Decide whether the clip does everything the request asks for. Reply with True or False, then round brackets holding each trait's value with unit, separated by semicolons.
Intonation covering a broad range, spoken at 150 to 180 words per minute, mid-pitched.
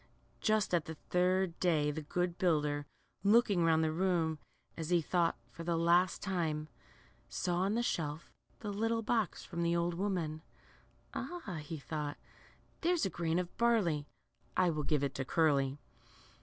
False (3.4 semitones; 160 wpm; 170 Hz)